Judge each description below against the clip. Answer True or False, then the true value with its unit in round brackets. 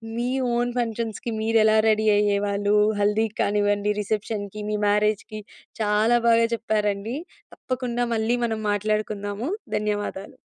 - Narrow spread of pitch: True (1.7 semitones)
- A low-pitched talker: False (215 Hz)